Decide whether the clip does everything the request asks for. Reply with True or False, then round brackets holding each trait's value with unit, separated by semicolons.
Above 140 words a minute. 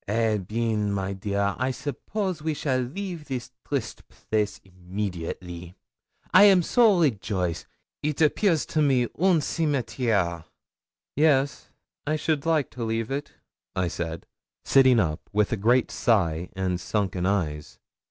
False (135 wpm)